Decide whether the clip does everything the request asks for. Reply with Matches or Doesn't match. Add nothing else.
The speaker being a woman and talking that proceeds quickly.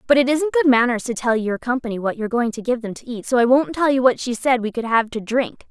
Matches